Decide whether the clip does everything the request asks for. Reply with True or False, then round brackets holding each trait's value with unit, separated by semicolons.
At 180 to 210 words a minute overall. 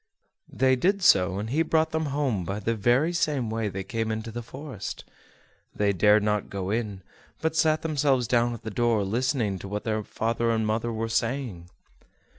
True (190 wpm)